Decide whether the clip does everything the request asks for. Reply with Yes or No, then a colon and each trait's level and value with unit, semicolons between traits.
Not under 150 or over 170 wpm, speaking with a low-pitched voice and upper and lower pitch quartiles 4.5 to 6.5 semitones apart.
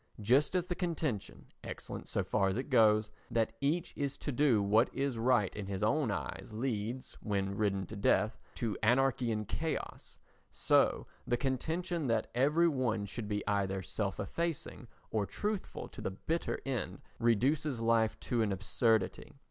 Yes: average, 165 wpm; low, 115 Hz; average, 5.1 semitones